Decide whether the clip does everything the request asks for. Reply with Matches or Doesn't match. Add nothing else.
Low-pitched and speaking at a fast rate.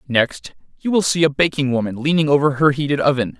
Doesn't match